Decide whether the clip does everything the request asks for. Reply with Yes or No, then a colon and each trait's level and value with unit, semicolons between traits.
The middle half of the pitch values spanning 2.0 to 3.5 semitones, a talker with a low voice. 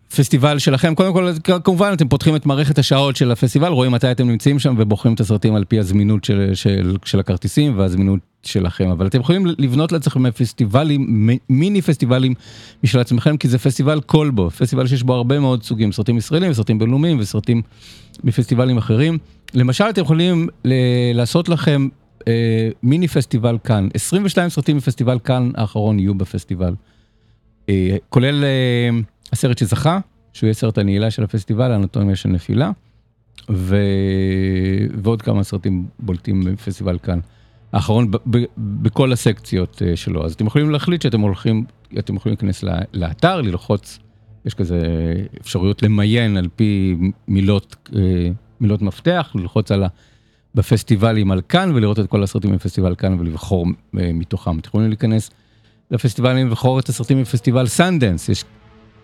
No: average, 4.5 semitones; low, 115 Hz